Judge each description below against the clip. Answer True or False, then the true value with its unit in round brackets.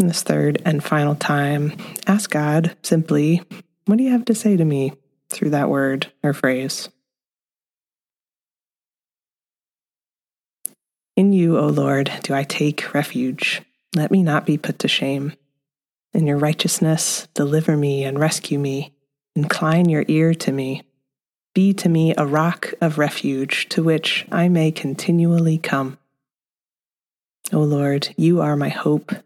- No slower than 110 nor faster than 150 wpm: True (140 wpm)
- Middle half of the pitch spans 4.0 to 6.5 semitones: False (3.2 semitones)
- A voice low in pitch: False (155 Hz)